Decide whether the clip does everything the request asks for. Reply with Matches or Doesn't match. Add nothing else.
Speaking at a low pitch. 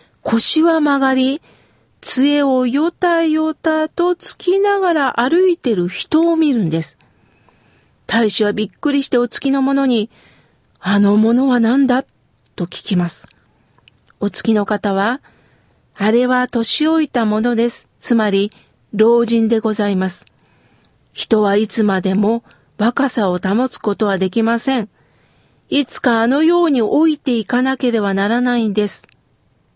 Doesn't match